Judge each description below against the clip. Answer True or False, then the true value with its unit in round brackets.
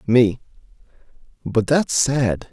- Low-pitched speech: True (120 Hz)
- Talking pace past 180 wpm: False (95 wpm)